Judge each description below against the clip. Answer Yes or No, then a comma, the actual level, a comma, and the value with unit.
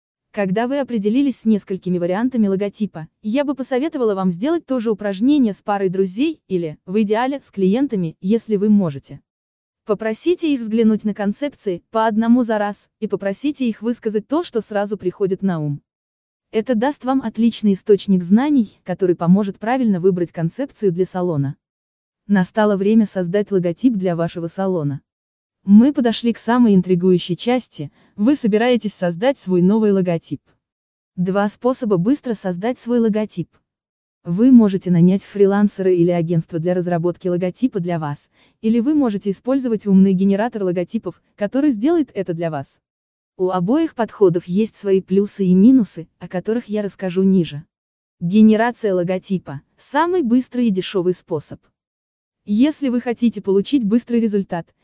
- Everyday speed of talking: Yes, average, 145 wpm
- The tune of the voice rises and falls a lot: No, average, 4.3 semitones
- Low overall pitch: No, high, 205 Hz